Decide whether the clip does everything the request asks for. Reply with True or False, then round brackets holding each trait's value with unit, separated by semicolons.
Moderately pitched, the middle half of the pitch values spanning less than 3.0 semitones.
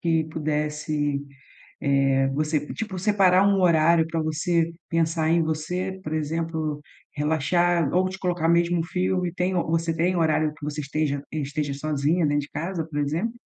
True (160 Hz; 2.6 semitones)